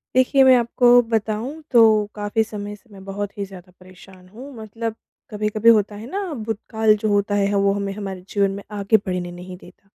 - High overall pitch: Yes, high, 205 Hz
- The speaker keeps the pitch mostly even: Yes, narrow, 2.3 semitones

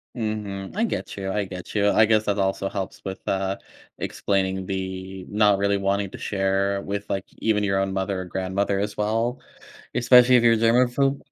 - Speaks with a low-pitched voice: Yes, low, 100 Hz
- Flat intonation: Yes, narrow, 2.0 semitones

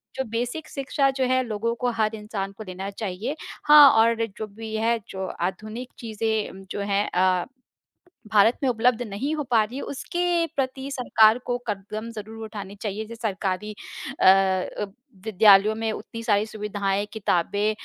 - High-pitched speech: Yes, high, 220 Hz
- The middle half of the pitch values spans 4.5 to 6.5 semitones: No, average, 3.0 semitones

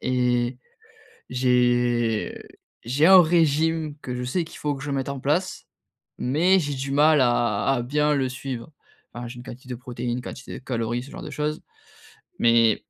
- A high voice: No, low, 130 Hz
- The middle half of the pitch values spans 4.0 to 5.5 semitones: No, average, 3.4 semitones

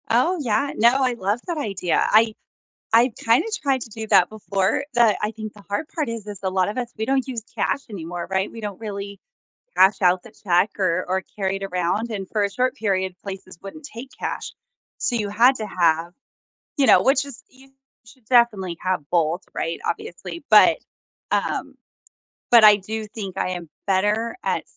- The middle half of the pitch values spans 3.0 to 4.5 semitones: Yes, average, 3.9 semitones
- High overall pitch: Yes, high, 210 Hz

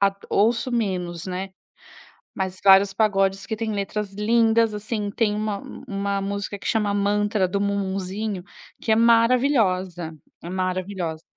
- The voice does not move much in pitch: Yes, narrow, 2.3 semitones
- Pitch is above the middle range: Yes, high, 200 Hz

